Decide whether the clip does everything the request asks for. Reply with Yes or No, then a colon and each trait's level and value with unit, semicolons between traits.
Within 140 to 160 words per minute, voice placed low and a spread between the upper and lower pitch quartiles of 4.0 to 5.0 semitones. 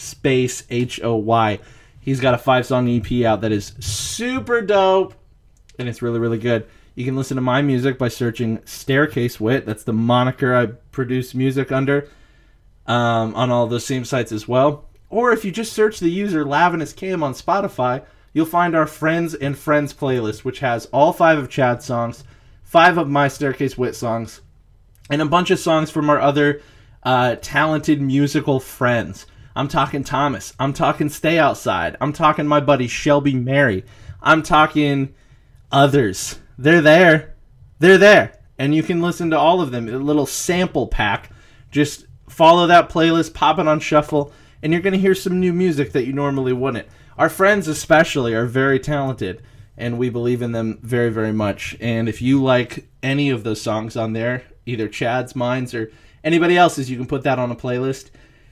No: average, 185 wpm; low, 130 Hz; average, 4.4 semitones